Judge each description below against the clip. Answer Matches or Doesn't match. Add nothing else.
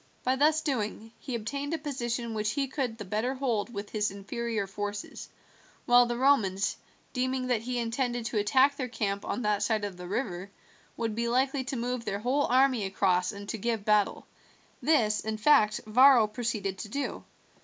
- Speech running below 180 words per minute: Doesn't match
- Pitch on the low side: Doesn't match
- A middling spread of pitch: Matches